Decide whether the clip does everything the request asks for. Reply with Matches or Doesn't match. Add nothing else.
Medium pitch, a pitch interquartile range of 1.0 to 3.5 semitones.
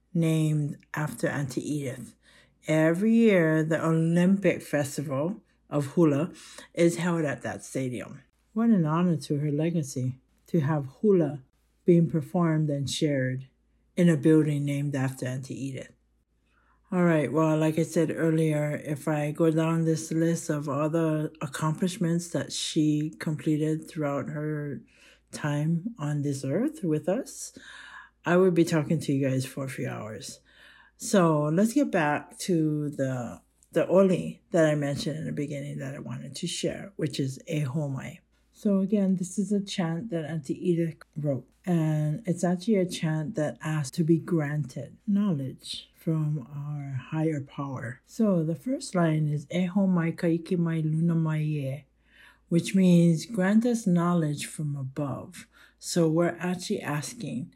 Matches